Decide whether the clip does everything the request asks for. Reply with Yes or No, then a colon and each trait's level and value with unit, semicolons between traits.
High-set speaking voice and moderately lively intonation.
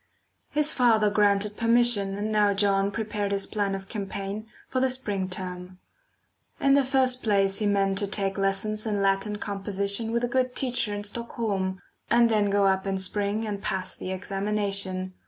No: high, 205 Hz; narrow, 2.2 semitones